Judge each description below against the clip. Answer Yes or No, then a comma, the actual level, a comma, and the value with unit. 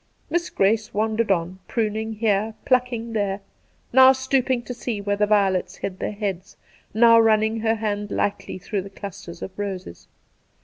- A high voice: Yes, high, 215 Hz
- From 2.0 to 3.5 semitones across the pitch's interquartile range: Yes, narrow, 2.4 semitones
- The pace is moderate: Yes, average, 160 wpm